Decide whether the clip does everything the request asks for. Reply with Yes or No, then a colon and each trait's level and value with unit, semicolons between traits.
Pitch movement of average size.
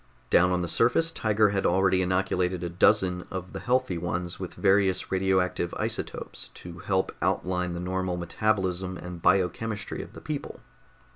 No: narrow, 1.7 semitones